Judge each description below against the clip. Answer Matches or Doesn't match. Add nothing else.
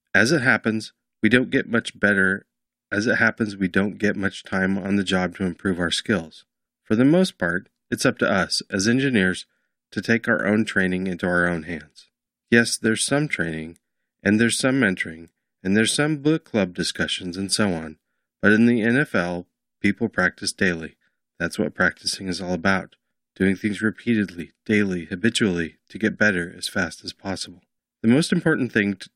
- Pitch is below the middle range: Matches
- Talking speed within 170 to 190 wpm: Matches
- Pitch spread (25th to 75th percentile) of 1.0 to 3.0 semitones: Doesn't match